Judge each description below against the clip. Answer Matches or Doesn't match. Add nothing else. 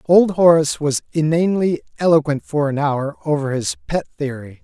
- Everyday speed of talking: Matches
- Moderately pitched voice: Matches